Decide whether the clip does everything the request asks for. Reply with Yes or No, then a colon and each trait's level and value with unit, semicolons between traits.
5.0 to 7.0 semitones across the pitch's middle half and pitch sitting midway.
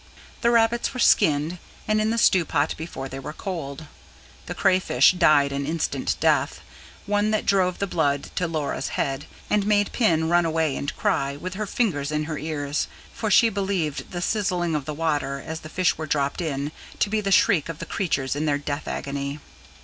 Yes: average, 5.3 semitones; medium, 160 Hz